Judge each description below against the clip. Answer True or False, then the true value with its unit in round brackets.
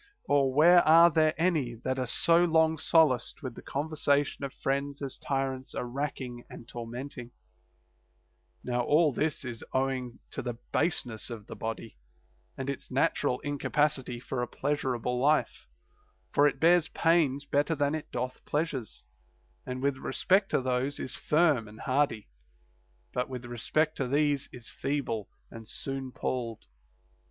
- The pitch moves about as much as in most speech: True (3.3 semitones)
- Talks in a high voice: False (135 Hz)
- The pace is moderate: True (155 wpm)